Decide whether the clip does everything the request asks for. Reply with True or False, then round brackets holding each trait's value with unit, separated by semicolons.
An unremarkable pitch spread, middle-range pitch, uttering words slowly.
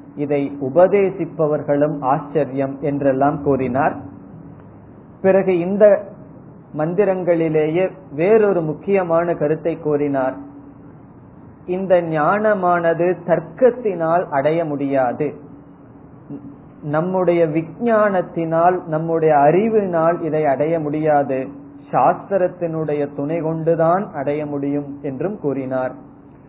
True (3.7 semitones; 160 Hz; 70 wpm)